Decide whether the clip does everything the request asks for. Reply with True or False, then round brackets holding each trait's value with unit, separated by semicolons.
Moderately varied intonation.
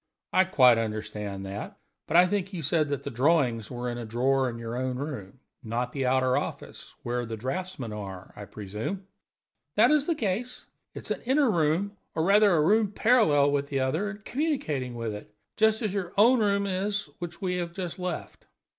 False (8.5 semitones)